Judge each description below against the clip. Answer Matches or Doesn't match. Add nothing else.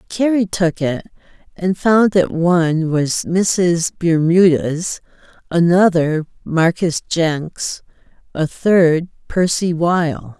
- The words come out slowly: Matches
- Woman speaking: Matches